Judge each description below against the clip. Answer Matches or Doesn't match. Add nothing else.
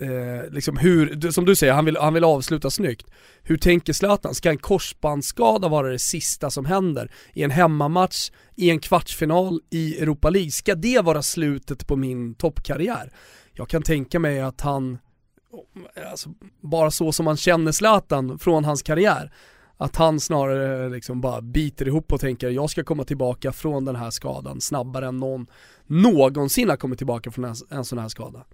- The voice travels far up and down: Doesn't match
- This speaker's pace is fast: Doesn't match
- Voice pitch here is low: Doesn't match